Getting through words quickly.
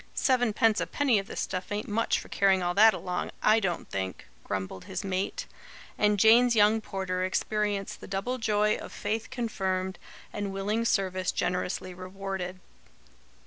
No: average, 155 wpm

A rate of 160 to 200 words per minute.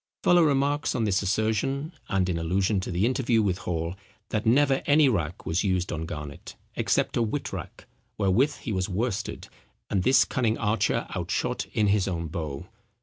Yes: average, 170 wpm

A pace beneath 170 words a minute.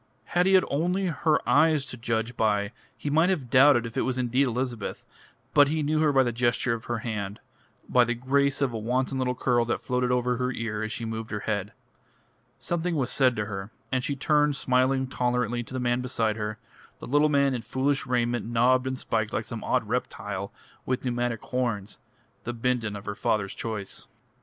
No: fast, 205 wpm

